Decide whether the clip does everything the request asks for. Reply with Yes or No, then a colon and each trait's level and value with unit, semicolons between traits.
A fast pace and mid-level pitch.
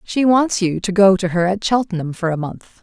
No: fast, 255 wpm; high, 195 Hz